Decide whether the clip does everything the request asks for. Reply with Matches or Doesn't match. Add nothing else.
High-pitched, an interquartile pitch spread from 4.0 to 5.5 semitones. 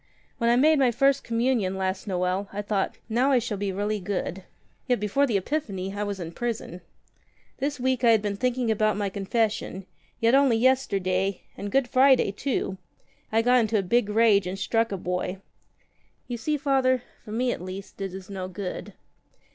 Matches